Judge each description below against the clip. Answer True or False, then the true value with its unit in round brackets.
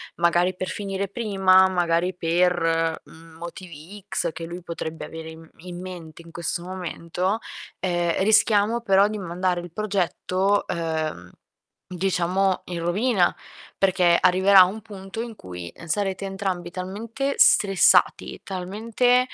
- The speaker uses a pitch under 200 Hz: True (185 Hz)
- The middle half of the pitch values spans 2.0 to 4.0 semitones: True (2.6 semitones)